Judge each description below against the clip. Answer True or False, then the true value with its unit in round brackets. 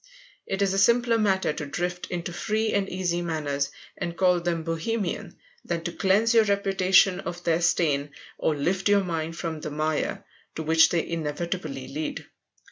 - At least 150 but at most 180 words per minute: True (170 wpm)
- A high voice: False (175 Hz)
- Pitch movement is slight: False (3.3 semitones)